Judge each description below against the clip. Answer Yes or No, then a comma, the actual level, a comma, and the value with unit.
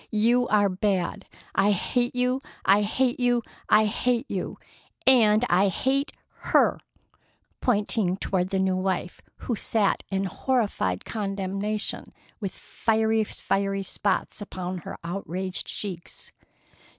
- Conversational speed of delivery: No, slow, 115 wpm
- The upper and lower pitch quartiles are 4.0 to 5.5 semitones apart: No, average, 3.3 semitones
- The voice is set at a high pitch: Yes, high, 205 Hz